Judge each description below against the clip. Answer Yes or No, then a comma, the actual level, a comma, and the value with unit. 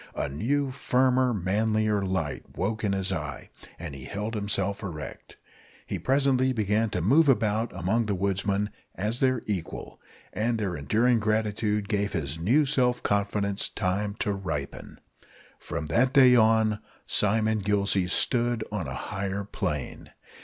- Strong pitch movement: No, average, 3.3 semitones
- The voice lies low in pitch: Yes, low, 105 Hz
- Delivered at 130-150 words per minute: Yes, average, 140 wpm